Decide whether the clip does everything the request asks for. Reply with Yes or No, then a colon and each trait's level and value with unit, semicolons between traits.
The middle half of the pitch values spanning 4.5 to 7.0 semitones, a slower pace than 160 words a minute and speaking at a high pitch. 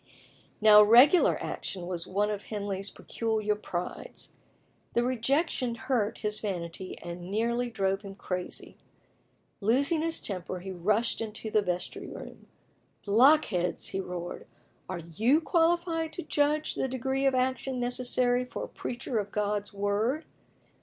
Yes: average, 4.9 semitones; average, 140 wpm; high, 220 Hz